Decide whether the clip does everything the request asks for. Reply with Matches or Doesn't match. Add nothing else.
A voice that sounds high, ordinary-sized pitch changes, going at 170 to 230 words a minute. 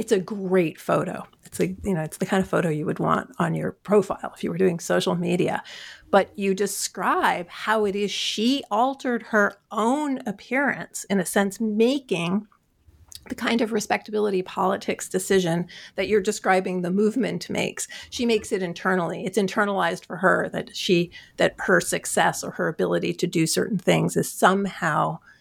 Matches